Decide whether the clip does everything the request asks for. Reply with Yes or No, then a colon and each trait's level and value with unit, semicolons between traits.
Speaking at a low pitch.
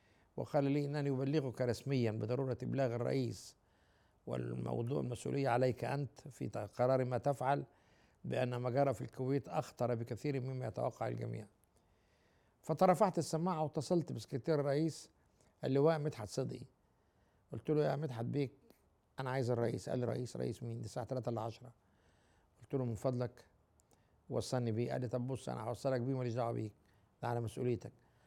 Yes: low, 125 Hz